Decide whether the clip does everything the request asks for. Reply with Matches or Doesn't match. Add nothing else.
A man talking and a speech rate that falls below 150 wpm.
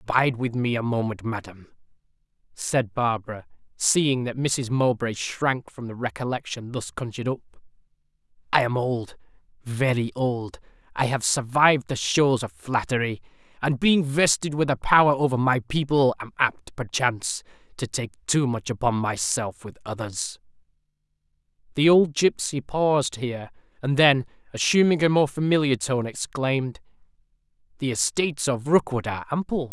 Matches